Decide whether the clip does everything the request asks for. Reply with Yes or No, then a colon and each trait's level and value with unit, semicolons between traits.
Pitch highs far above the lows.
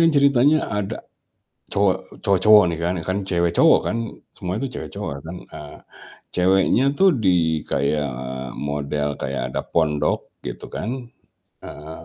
Yes: wide, 6.0 semitones